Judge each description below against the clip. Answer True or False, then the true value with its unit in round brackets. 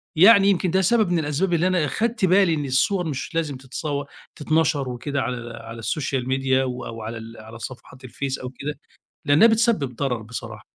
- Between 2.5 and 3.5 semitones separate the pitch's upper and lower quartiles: False (5.5 semitones)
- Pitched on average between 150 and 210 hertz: False (140 Hz)